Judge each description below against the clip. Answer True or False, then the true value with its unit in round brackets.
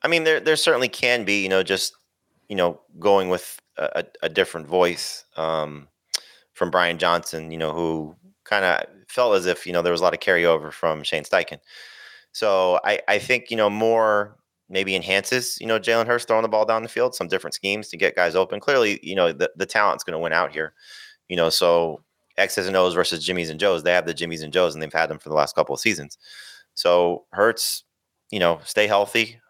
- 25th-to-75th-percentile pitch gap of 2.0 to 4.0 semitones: False (4.7 semitones)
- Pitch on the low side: True (95 Hz)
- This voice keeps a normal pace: False (225 wpm)